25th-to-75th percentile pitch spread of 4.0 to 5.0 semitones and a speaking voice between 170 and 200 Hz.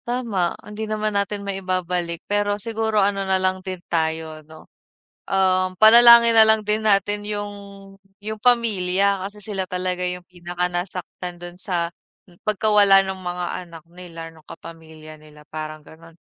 No: average, 3.1 semitones; medium, 185 Hz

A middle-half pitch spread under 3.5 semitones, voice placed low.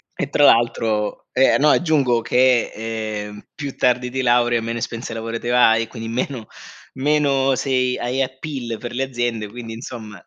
Yes: narrow, 2.6 semitones; low, 120 Hz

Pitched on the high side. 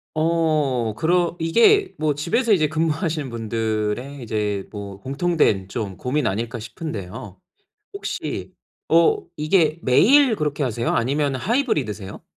No: medium, 145 Hz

